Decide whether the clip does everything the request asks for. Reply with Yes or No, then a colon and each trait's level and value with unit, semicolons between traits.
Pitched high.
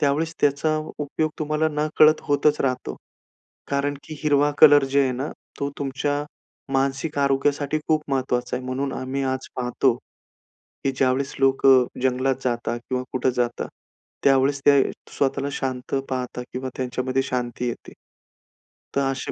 No: low, 135 Hz